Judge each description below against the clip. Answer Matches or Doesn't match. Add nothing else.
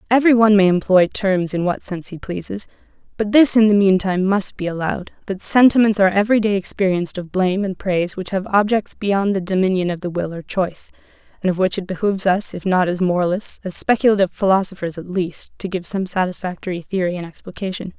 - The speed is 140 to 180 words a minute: Doesn't match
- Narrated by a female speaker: Matches